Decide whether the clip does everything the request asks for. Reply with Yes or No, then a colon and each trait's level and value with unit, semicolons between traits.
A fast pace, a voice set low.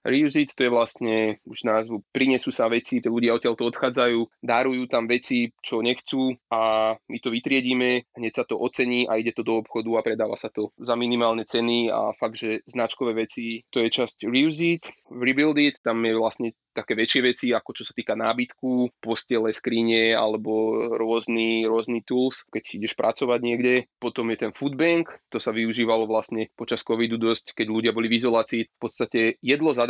Yes: fast, 185 wpm; low, 115 Hz